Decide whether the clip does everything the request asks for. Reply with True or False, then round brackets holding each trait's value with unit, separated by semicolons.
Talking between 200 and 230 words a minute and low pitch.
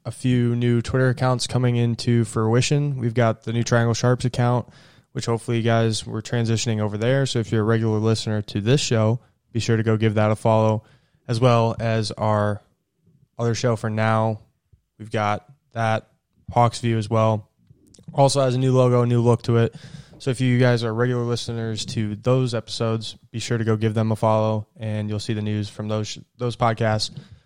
True (205 wpm; 115 Hz)